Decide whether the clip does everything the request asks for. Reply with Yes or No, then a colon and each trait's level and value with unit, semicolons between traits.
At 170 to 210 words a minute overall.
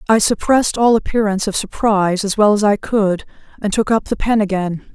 Yes: fast, 205 wpm